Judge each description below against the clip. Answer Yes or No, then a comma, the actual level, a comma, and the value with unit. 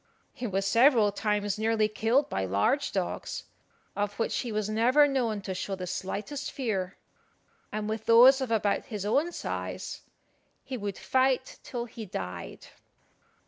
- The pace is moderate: Yes, average, 150 wpm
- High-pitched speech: Yes, high, 220 Hz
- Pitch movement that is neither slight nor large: Yes, average, 4.0 semitones